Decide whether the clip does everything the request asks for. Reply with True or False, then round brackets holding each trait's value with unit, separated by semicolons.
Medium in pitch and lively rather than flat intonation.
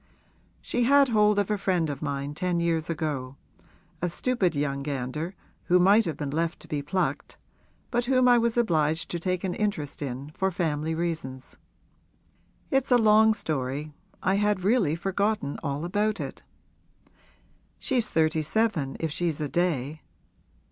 True (170 Hz; 5.8 semitones)